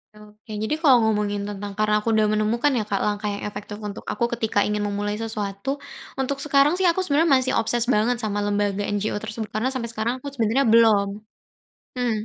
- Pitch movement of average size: Yes, average, 3.0 semitones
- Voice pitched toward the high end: Yes, high, 215 Hz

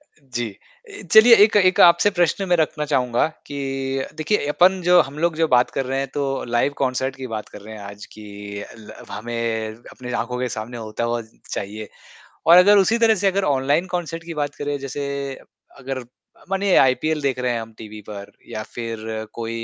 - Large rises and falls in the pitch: Yes, wide, 6.9 semitones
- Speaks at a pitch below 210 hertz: Yes, low, 135 Hz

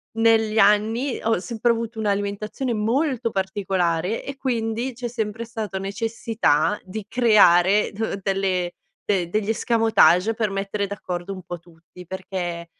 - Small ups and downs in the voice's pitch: No, average, 3.2 semitones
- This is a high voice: Yes, high, 210 Hz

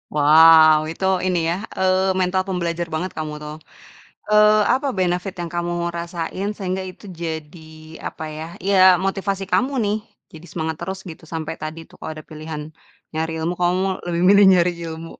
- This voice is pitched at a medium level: Yes, medium, 175 Hz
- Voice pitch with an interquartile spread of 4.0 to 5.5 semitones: No, average, 2.8 semitones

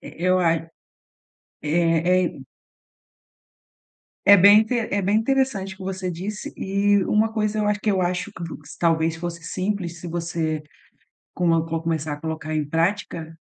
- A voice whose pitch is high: No, medium, 180 Hz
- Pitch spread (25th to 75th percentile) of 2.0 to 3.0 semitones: No, average, 3.7 semitones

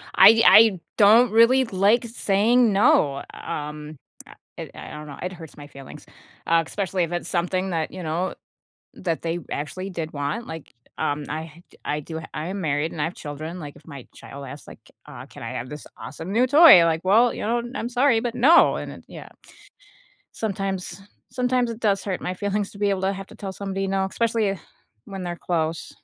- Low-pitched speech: No, medium, 185 Hz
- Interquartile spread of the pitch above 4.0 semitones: Yes, average, 5.1 semitones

